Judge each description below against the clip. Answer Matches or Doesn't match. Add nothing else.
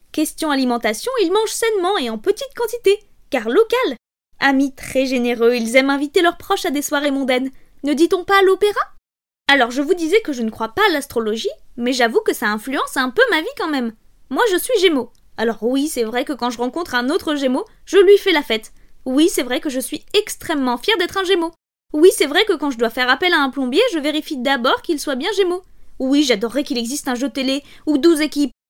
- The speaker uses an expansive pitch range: Matches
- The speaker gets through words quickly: Matches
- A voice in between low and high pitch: Doesn't match